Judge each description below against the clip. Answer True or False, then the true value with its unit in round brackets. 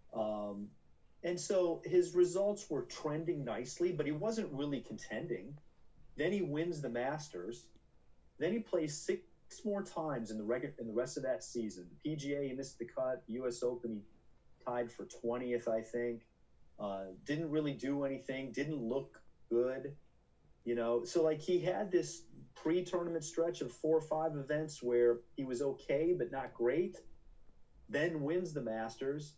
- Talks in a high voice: False (140 Hz)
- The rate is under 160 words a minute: False (165 wpm)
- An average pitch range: False (5.7 semitones)